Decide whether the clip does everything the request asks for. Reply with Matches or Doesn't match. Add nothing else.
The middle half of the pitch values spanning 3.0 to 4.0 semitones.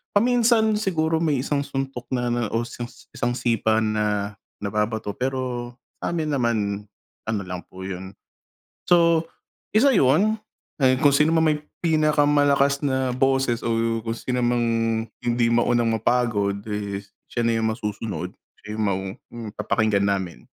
Doesn't match